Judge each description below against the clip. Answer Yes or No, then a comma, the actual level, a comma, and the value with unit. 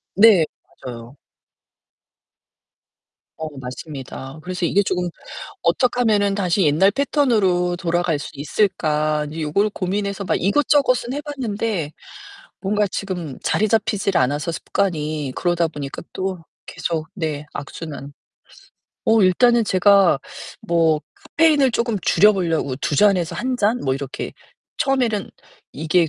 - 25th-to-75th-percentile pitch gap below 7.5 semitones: Yes, average, 5.2 semitones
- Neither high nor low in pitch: Yes, medium, 180 Hz